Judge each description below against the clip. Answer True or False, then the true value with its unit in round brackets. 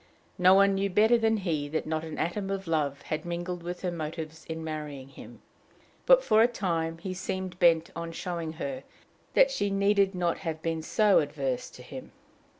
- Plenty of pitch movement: False (3.6 semitones)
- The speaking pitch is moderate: True (175 Hz)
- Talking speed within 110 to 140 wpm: False (190 wpm)